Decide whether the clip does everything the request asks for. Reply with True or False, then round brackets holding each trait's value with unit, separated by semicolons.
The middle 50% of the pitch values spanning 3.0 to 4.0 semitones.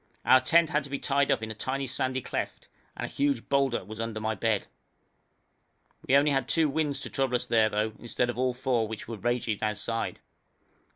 True (3.7 semitones)